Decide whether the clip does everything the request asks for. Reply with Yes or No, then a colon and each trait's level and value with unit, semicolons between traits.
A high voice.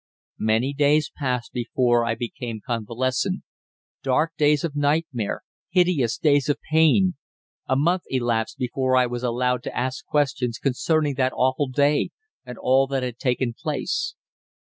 No: low, 130 Hz